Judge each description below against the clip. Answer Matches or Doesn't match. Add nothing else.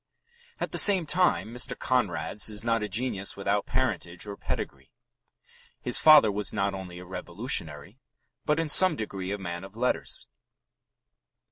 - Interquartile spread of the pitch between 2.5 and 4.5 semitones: Doesn't match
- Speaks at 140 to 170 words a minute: Matches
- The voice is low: Matches